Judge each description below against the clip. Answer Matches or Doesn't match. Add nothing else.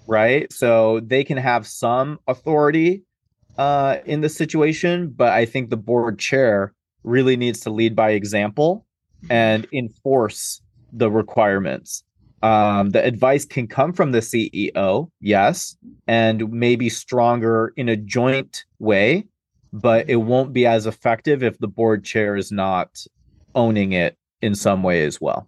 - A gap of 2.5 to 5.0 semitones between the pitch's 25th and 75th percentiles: Matches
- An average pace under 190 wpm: Matches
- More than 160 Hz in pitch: Doesn't match